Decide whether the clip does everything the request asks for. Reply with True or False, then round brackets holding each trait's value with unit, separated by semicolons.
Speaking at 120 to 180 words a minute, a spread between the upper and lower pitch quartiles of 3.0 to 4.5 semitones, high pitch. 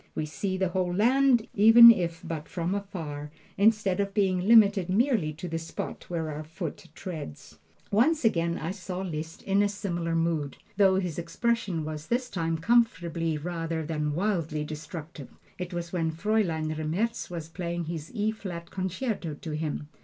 False (165 wpm; 3.9 semitones; 175 Hz)